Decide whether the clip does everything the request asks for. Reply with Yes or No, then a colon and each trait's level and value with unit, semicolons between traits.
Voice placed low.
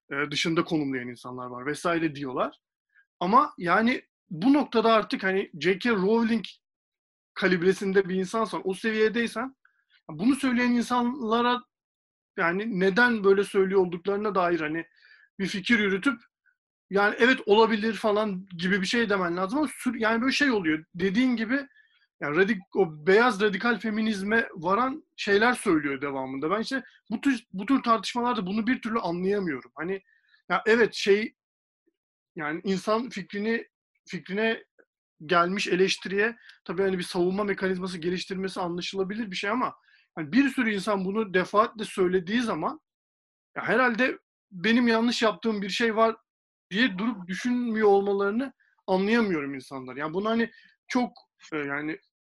No: high, 205 Hz